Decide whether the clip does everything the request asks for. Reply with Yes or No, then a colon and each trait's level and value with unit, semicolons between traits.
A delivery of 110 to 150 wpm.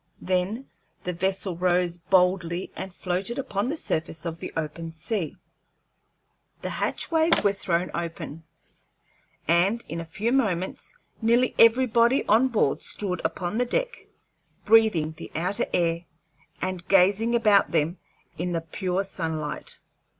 Yes: slow, 135 wpm